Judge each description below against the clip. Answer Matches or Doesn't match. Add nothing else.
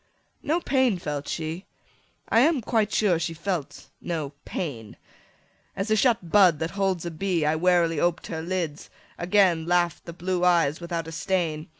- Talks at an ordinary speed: Matches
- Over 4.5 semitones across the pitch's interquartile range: Doesn't match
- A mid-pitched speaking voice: Matches